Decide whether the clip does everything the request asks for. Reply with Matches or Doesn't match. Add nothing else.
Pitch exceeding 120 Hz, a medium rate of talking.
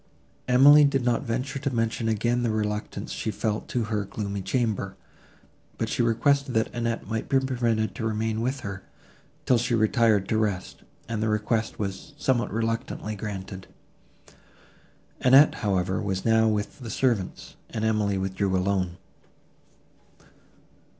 Doesn't match